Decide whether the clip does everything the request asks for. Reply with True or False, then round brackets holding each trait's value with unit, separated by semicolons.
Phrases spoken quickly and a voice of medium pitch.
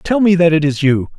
True (305 wpm; 165 Hz)